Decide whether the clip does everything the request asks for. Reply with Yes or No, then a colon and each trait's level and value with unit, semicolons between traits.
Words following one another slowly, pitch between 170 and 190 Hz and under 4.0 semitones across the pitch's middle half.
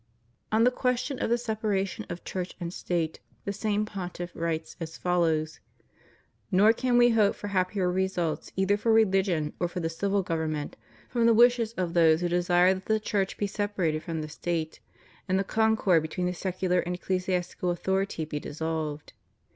No: average, 175 wpm; medium, 185 Hz; average, 3.5 semitones